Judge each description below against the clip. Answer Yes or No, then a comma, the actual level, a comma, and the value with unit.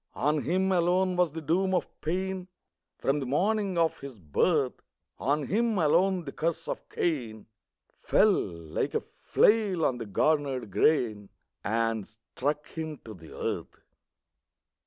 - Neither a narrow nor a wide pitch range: No, wide, 6.8 semitones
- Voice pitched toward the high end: No, medium, 155 Hz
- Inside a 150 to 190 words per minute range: No, average, 140 wpm